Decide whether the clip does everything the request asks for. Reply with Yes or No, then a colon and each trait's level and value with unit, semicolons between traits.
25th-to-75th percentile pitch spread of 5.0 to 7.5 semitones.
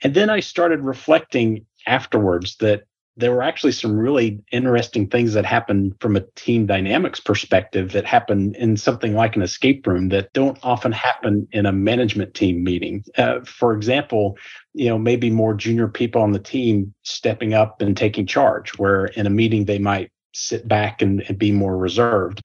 No: average, 2.9 semitones